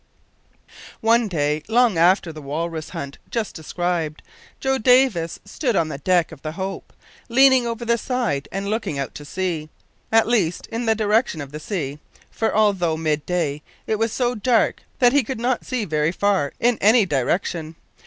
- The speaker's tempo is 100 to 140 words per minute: No, average, 175 wpm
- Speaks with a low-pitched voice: No, high, 190 Hz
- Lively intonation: Yes, wide, 6.6 semitones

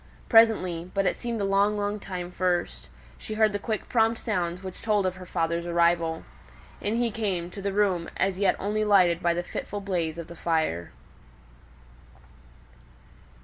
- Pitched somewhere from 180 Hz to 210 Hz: Yes, high, 190 Hz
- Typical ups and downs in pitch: Yes, average, 3.3 semitones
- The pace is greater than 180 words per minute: No, average, 170 wpm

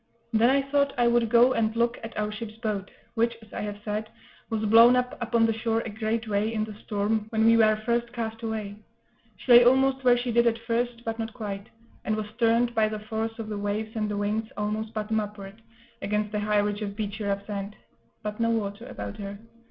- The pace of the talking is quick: Yes, fast, 225 wpm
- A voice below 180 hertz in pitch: No, high, 220 Hz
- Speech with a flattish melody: Yes, narrow, 1.8 semitones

